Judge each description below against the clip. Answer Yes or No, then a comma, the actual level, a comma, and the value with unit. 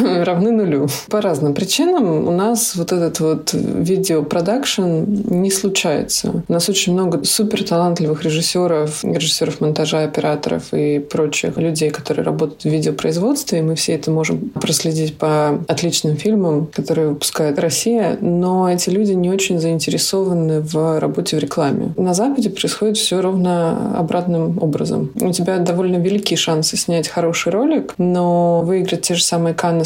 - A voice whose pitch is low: No, medium, 170 Hz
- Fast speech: No, average, 145 wpm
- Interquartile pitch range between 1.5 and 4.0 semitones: Yes, average, 3.1 semitones